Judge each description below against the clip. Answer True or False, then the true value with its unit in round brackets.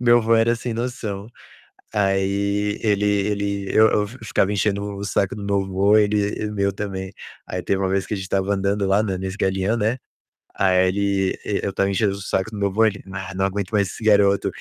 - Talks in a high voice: False (100 Hz)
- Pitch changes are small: True (1.4 semitones)